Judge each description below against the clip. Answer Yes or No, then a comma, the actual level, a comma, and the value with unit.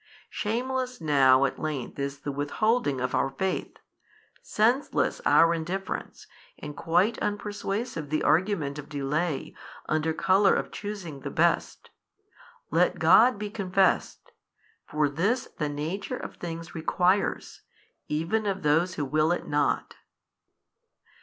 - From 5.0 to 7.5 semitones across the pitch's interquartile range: Yes, wide, 5.4 semitones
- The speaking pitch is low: No, medium, 165 Hz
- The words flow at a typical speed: No, slow, 125 wpm